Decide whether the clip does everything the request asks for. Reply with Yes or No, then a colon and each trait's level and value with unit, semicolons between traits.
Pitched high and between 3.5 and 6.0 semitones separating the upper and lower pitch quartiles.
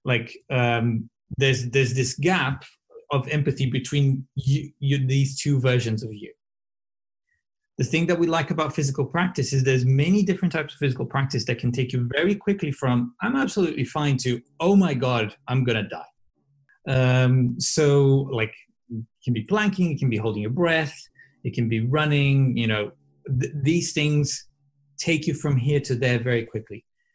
No: medium, 140 Hz; average, 3.8 semitones